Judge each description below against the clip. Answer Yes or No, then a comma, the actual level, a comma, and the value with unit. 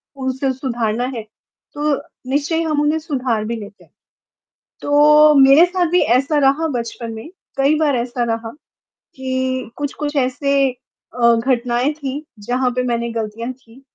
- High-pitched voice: Yes, very high, 260 Hz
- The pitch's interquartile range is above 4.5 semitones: No, average, 3.6 semitones